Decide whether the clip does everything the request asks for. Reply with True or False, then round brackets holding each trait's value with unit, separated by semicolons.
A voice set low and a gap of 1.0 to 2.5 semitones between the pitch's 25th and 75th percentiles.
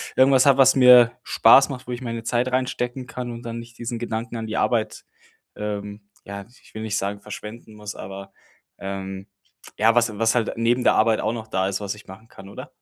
False (115 Hz; 2.9 semitones)